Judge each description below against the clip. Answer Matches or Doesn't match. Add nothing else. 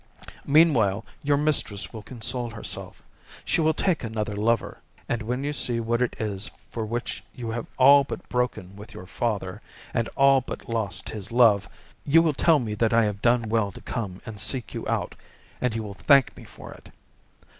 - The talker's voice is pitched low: Matches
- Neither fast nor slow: Matches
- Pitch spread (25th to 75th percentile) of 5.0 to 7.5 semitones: Doesn't match